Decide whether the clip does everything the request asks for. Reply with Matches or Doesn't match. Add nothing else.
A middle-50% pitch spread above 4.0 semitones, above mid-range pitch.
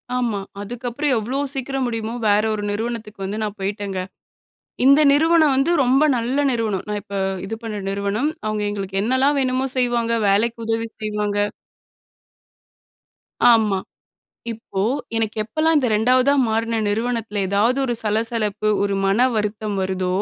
Doesn't match